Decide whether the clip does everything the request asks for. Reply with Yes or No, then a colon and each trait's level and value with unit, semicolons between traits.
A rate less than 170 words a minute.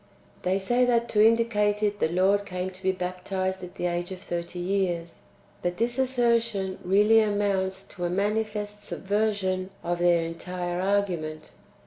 Yes: average, 155 wpm